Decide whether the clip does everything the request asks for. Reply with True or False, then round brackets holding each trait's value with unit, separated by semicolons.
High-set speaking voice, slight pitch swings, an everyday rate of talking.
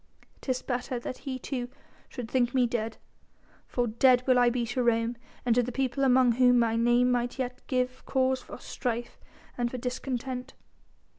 True (245 Hz; 1.2 semitones; 175 wpm)